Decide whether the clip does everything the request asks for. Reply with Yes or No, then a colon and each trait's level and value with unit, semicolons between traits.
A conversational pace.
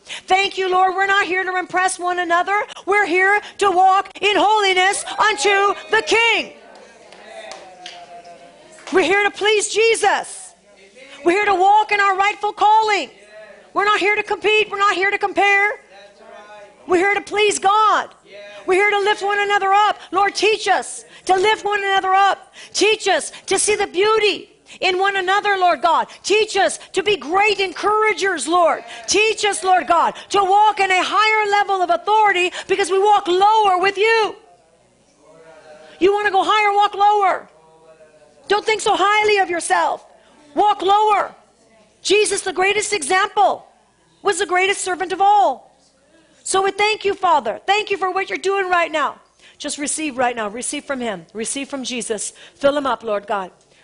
Yes: average, 170 wpm